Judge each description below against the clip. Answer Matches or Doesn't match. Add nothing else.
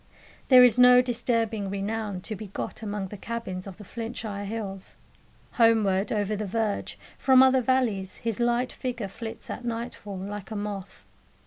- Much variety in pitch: Doesn't match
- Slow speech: Doesn't match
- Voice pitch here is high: Matches